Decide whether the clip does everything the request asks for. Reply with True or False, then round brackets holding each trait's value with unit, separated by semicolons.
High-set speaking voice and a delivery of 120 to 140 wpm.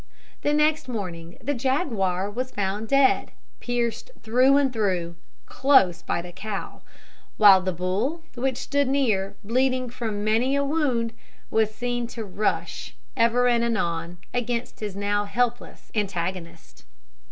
True (230 Hz; 135 wpm)